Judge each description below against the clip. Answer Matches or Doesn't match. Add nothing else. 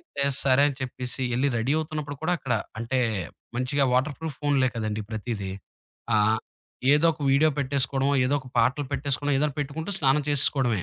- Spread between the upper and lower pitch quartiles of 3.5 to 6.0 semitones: Doesn't match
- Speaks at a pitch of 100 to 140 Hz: Matches